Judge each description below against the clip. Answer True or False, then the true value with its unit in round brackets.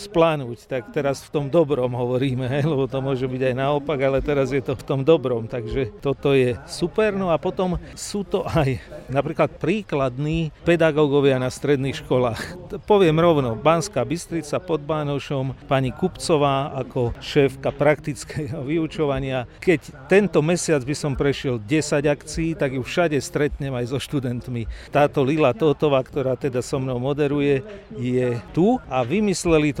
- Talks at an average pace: True (155 wpm)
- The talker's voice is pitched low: False (145 Hz)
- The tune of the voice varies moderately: True (3.2 semitones)